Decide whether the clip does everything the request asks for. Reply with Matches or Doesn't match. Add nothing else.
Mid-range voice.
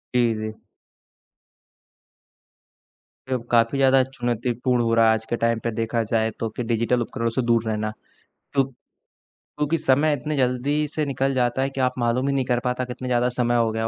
Doesn't match